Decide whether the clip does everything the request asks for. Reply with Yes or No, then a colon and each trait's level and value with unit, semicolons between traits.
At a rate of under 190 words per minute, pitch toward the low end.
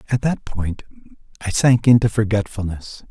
Yes: slow, 135 wpm; low, 110 Hz